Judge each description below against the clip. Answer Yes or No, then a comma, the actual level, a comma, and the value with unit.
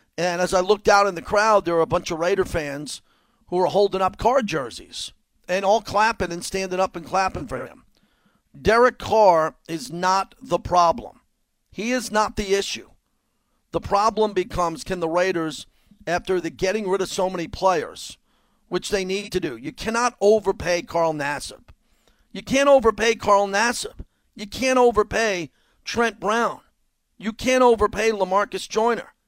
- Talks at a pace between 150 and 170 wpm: Yes, average, 165 wpm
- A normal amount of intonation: Yes, average, 3.7 semitones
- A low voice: No, high, 195 Hz